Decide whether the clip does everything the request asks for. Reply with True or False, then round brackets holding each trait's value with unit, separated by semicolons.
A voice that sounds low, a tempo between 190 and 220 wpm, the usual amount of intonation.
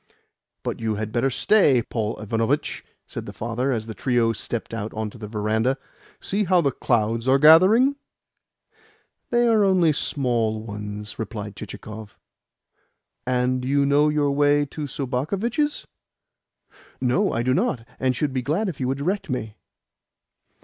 False (130 Hz; 150 wpm; 5.0 semitones)